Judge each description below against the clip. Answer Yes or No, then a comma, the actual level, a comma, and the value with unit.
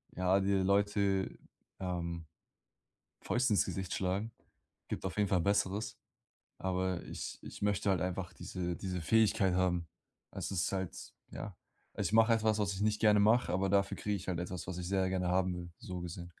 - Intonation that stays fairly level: Yes, narrow, 2.1 semitones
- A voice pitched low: Yes, very low, 95 Hz